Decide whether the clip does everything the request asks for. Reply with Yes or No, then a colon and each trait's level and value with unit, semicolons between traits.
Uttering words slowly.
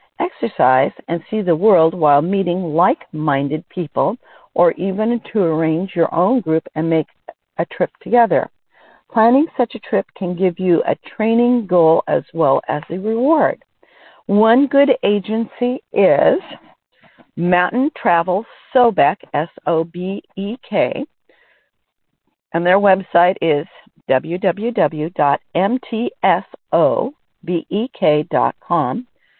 Yes: slow, 110 wpm